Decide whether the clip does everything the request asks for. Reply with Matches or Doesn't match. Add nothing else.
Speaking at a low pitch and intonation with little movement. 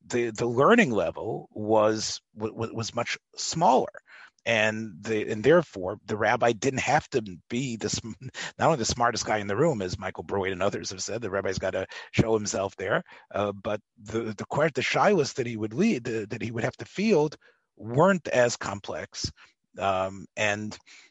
Matches